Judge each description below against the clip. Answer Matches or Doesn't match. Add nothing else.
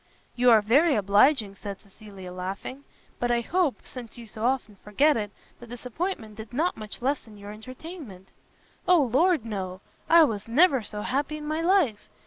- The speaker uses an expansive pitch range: Matches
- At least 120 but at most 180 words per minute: Matches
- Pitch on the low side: Doesn't match